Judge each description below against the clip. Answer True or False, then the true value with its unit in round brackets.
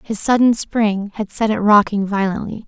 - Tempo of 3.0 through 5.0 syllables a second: True (4.8 syllables/s)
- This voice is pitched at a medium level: False (210 Hz)